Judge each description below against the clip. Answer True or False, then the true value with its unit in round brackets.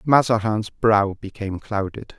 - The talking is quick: False (110 wpm)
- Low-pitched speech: True (105 Hz)